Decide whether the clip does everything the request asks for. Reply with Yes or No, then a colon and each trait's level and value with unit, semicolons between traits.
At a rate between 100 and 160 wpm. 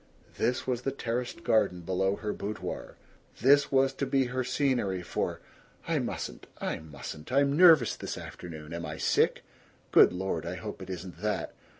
No: average, 170 wpm